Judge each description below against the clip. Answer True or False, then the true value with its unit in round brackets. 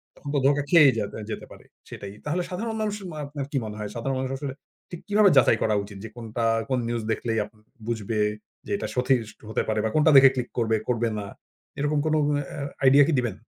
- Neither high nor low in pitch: False (130 Hz)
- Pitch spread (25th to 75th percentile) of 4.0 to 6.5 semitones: True (4.7 semitones)